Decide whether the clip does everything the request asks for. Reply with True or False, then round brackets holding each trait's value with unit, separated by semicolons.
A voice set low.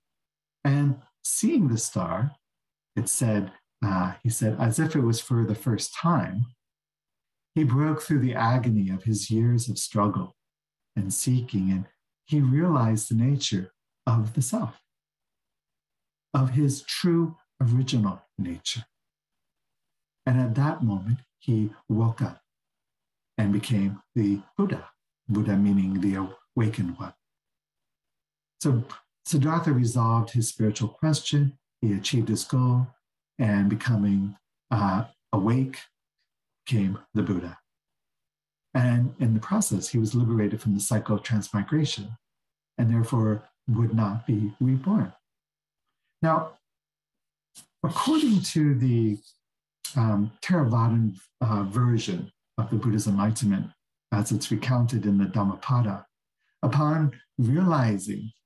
True (115 Hz)